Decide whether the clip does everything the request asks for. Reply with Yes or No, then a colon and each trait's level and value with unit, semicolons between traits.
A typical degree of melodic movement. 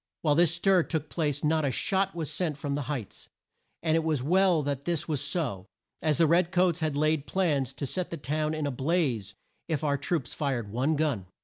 Yes: average, 3.1 semitones